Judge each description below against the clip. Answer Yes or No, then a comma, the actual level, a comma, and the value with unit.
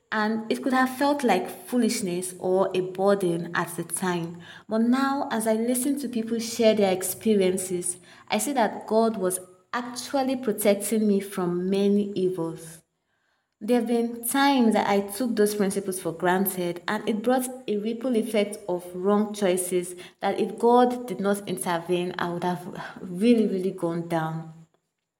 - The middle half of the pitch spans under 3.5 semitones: No, average, 3.9 semitones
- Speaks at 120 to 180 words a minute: Yes, average, 160 wpm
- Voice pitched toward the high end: Yes, high, 200 Hz